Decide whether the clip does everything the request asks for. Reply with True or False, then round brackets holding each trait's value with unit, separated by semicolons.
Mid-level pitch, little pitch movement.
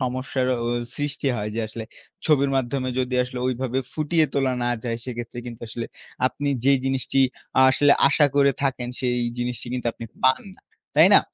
False (130 Hz; 2.2 semitones)